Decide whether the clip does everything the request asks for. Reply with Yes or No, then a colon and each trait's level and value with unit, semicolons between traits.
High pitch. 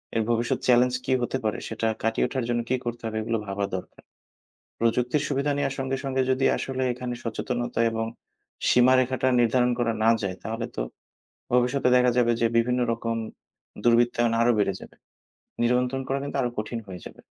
No: low, 120 Hz